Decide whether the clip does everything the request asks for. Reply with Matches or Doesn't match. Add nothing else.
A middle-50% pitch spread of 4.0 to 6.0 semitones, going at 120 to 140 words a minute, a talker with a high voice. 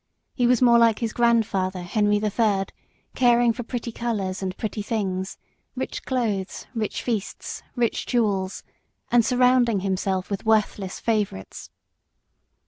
Doesn't match